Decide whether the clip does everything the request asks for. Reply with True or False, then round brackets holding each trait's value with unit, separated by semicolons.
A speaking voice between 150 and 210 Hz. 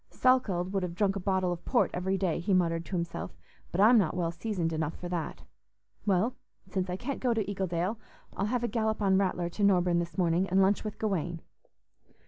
True (190 Hz)